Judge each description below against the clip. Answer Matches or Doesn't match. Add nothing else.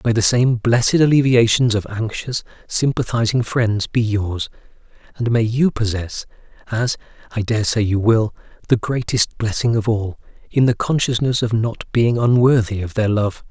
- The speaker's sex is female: Doesn't match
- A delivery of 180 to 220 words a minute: Doesn't match